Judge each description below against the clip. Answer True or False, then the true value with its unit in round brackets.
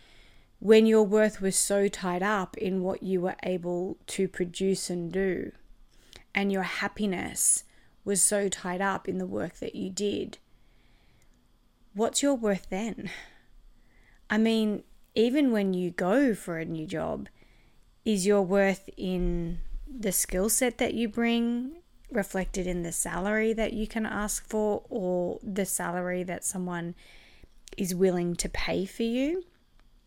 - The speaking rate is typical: True (145 wpm)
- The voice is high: True (195 Hz)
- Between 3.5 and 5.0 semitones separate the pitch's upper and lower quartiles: False (3.1 semitones)